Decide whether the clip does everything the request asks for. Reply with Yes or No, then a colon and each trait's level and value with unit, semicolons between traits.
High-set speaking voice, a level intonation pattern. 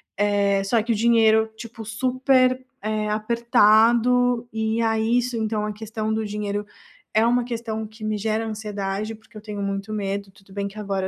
Yes: high, 220 Hz; narrow, 1.9 semitones